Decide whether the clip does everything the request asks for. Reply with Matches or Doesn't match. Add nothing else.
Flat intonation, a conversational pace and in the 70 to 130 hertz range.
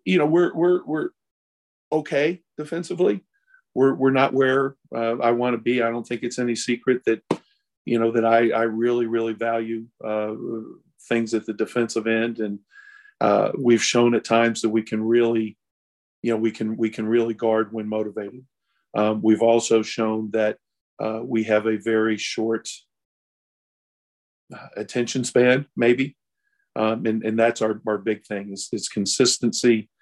Matches